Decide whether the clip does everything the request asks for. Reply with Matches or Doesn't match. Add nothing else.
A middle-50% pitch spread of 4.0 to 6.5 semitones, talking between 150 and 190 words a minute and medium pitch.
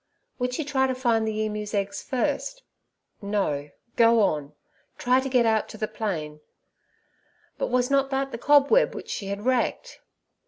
Doesn't match